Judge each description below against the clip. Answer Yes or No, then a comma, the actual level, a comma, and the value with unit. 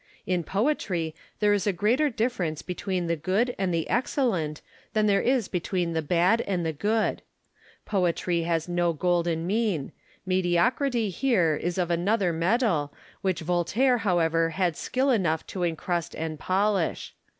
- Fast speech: No, average, 150 wpm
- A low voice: No, medium, 180 Hz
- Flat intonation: No, average, 4.1 semitones